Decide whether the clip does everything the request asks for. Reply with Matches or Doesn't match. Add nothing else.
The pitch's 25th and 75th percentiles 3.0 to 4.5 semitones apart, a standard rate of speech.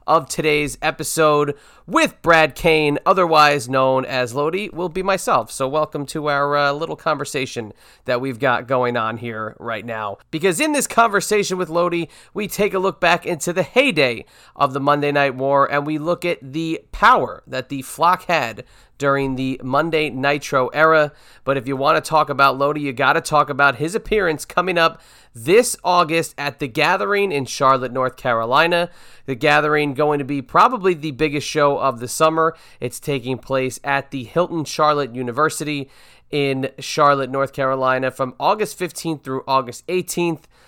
Matches